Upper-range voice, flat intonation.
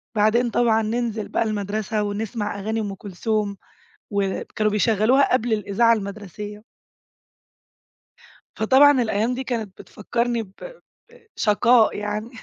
Yes: high, 215 Hz; narrow, 2.2 semitones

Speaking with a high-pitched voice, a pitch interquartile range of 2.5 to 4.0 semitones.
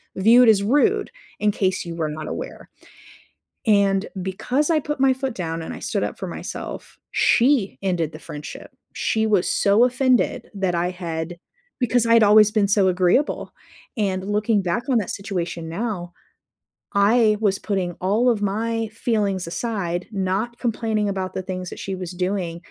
Yes: high, 200 Hz; average, 3.7 semitones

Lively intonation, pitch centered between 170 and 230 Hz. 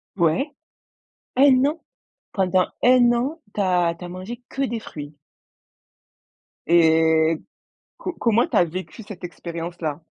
Yes: wide, 6.3 semitones; medium, 185 Hz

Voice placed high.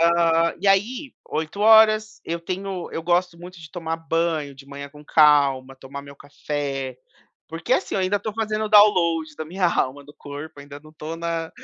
No: medium, 165 Hz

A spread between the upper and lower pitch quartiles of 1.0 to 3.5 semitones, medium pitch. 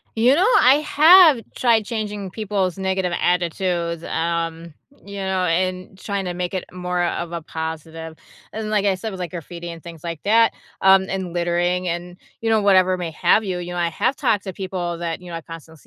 Yes: average, 2.8 semitones; medium, 180 Hz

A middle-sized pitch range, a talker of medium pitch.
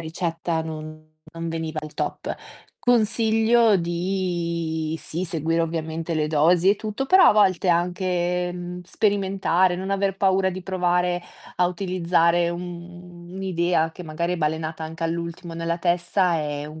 No: narrow, 2.2 semitones; medium, 175 Hz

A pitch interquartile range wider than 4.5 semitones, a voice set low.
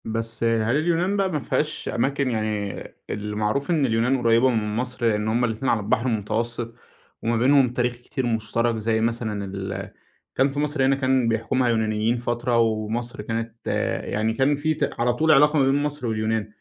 No: average, 3.2 semitones; low, 115 Hz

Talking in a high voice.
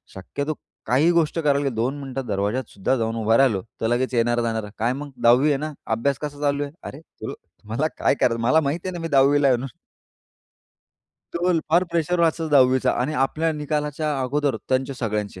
No: low, 135 Hz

